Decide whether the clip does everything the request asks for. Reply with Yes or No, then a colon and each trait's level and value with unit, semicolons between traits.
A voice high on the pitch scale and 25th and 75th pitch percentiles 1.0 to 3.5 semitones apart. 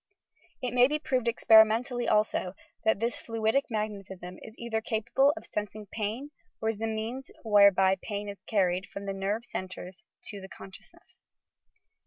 Yes: high, 215 Hz; average, 2.8 semitones